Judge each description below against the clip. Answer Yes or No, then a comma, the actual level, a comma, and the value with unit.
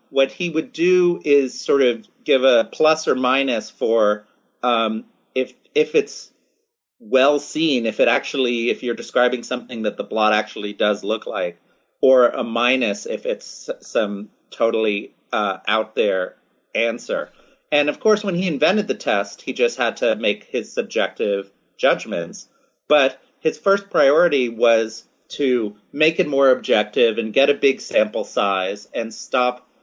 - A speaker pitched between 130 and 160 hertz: Yes, low, 135 Hz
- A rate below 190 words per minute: Yes, average, 155 wpm